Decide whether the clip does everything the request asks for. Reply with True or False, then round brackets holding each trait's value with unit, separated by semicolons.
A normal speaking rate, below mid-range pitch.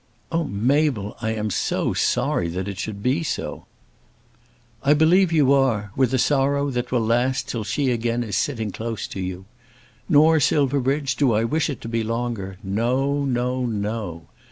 True (165 wpm; 120 Hz)